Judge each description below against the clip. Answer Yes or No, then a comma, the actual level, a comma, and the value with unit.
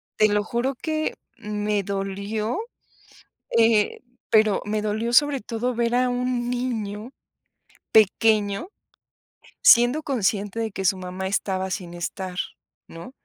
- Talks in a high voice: Yes, high, 215 Hz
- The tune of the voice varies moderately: Yes, average, 3.3 semitones